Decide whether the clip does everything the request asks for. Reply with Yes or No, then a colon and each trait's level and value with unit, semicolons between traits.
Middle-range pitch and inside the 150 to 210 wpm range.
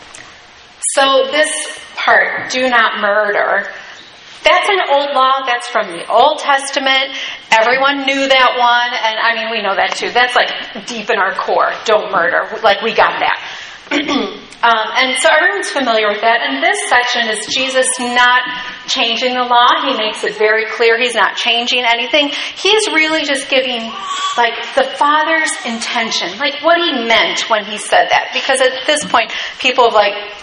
No: very high, 250 Hz; average, 170 wpm